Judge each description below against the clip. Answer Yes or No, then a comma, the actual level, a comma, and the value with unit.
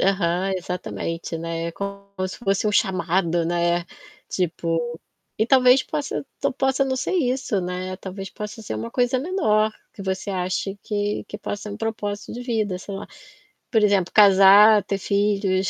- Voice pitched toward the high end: Yes, high, 200 Hz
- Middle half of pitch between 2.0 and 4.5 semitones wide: Yes, average, 3.0 semitones